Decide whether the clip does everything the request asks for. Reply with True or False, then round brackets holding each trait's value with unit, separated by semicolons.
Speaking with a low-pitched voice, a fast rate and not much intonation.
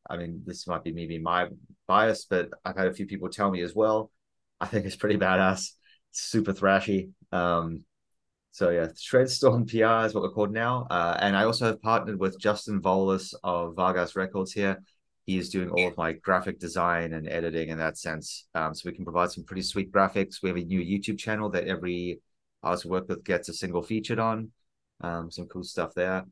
False (95 Hz; 210 wpm; 3.0 semitones)